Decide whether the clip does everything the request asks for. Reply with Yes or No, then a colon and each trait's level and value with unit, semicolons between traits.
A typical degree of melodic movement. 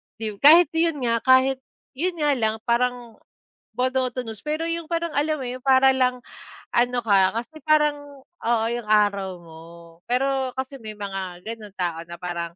Yes: average, 4.9 semitones